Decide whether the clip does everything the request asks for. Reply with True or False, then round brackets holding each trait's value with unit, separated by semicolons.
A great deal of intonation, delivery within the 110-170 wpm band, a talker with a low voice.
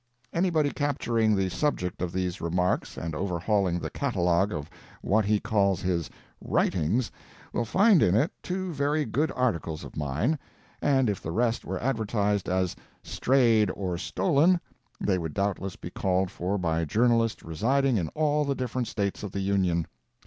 True (6.5 semitones; 160 wpm; 105 Hz)